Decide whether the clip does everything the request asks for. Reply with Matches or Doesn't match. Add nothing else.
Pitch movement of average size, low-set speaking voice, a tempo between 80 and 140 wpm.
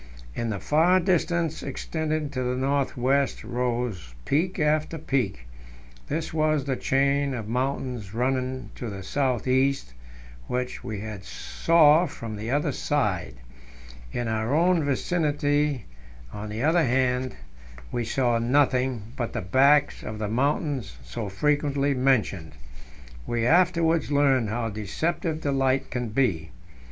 Matches